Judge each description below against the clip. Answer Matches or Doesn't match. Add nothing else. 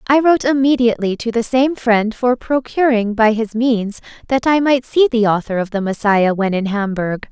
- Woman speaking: Matches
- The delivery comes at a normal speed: Matches